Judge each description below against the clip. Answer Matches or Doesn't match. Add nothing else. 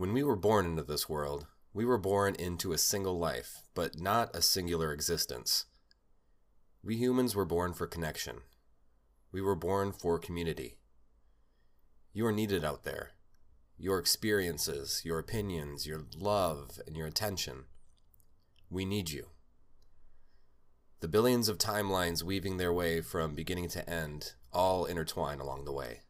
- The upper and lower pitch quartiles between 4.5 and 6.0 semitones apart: Matches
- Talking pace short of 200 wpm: Matches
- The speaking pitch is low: Matches